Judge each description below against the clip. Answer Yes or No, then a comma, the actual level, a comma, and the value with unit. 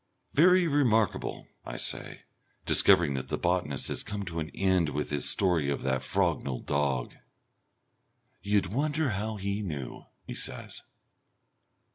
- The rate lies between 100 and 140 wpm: Yes, slow, 135 wpm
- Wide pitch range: Yes, wide, 6.8 semitones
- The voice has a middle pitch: No, very low, 90 Hz